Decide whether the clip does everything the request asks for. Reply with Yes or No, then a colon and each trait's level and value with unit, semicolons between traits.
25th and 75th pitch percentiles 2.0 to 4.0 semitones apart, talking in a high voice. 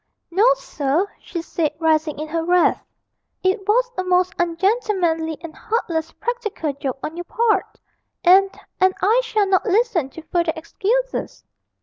No: average, 4.7 semitones; very high, 360 Hz